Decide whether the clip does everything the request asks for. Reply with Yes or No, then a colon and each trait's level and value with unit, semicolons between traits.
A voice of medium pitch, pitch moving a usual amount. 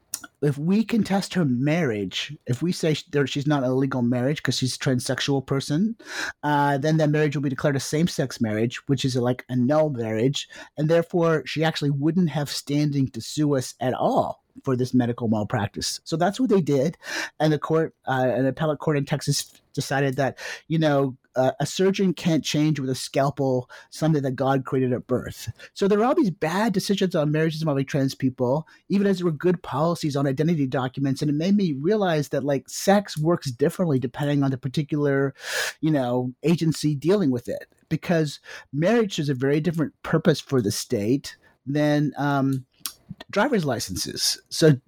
Yes: medium, 145 Hz; average, 3.3 semitones